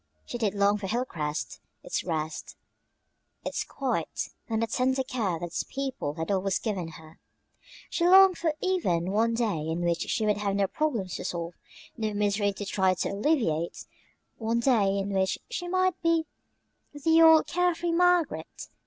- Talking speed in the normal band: Yes, average, 170 wpm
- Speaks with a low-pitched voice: No, high, 210 Hz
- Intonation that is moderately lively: No, wide, 8.4 semitones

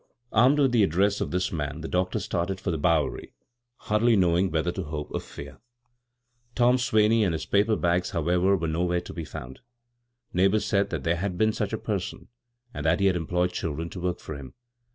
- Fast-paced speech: Yes, fast, 210 wpm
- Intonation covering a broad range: No, average, 3.4 semitones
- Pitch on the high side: No, very low, 90 Hz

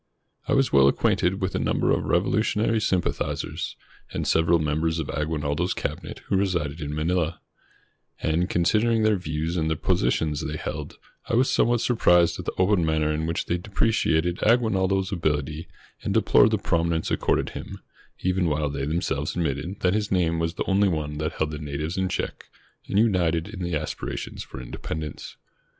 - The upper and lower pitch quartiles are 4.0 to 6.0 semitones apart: No, average, 3.6 semitones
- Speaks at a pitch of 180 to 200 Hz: No, very low, 85 Hz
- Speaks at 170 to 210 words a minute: Yes, average, 175 wpm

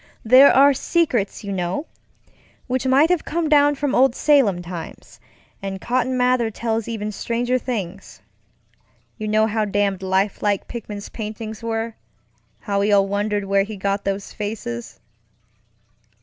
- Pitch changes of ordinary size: Yes, average, 4.2 semitones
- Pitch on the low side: No, high, 215 Hz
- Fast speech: No, slow, 135 wpm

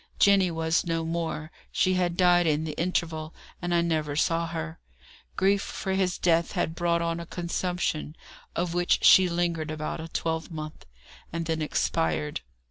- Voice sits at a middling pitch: Yes, medium, 165 Hz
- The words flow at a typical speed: Yes, average, 160 wpm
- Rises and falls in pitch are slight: Yes, narrow, 1.6 semitones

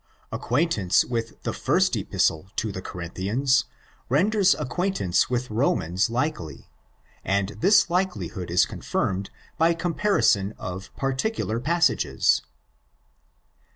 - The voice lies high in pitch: No, low, 120 Hz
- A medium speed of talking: No, slow, 100 wpm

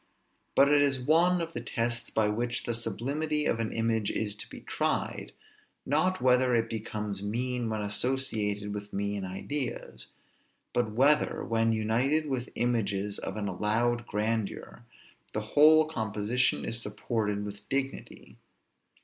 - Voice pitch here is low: Yes, low, 115 Hz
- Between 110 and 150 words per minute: Yes, average, 140 wpm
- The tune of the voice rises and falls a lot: No, average, 4.0 semitones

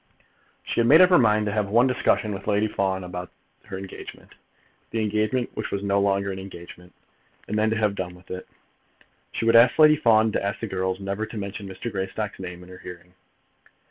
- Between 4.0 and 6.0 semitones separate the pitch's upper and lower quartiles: No, narrow, 2.5 semitones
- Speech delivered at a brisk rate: Yes, fast, 210 wpm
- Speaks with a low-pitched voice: Yes, low, 100 Hz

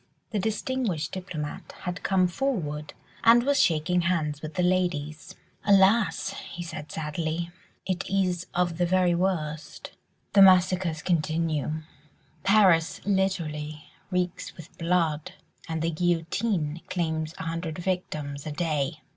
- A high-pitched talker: No, medium, 175 Hz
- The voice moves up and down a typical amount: Yes, average, 3.2 semitones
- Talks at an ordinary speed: No, slow, 125 wpm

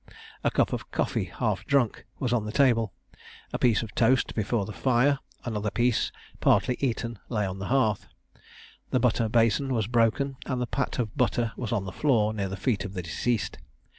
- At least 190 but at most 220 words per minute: Yes, average, 195 wpm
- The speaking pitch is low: Yes, low, 115 Hz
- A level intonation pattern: No, average, 3.0 semitones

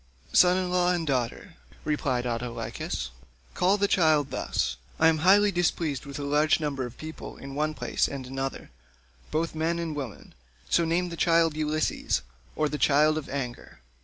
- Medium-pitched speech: Yes, medium, 155 Hz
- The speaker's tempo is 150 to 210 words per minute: Yes, average, 170 wpm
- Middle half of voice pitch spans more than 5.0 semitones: No, average, 3.5 semitones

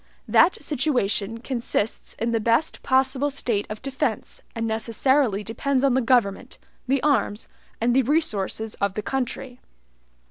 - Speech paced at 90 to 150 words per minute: Yes, average, 140 wpm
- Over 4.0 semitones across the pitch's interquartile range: No, average, 3.5 semitones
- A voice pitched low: No, high, 245 Hz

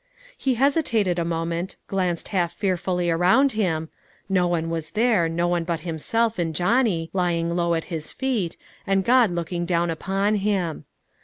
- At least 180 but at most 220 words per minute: No, average, 160 wpm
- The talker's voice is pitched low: No, medium, 175 Hz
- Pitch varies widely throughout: No, average, 3.5 semitones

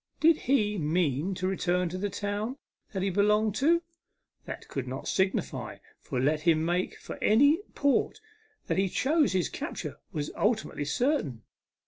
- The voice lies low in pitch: No, high, 190 Hz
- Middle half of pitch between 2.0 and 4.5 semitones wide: No, wide, 5.6 semitones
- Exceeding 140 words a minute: Yes, average, 155 wpm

